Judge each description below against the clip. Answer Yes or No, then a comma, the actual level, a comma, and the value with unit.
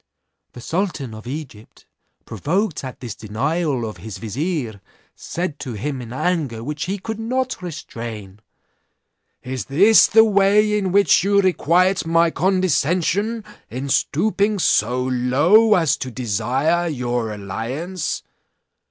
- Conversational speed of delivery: No, slow, 125 wpm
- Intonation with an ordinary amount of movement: No, wide, 7.6 semitones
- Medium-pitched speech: Yes, medium, 150 Hz